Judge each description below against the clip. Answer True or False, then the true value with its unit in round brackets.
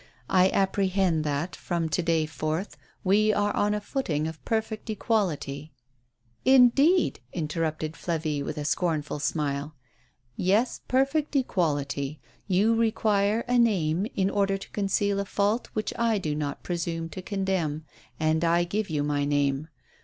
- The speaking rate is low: False (150 wpm)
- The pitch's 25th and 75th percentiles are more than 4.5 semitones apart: True (5.2 semitones)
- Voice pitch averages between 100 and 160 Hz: False (180 Hz)